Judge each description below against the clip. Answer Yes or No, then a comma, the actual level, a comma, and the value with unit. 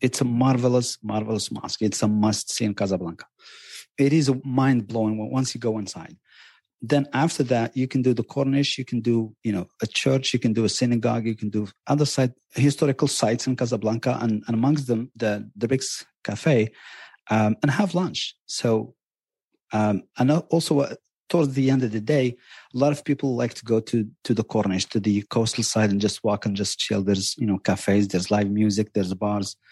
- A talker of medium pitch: No, low, 115 Hz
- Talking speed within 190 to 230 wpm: Yes, fast, 205 wpm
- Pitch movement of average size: Yes, average, 3.7 semitones